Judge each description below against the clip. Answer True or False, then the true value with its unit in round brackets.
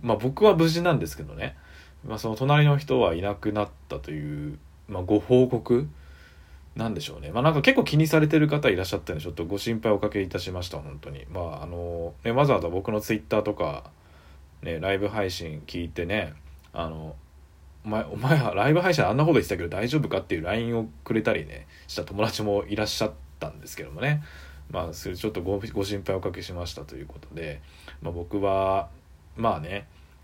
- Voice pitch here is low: True (90 Hz)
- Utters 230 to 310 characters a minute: False (405 characters per minute)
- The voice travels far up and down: True (6.2 semitones)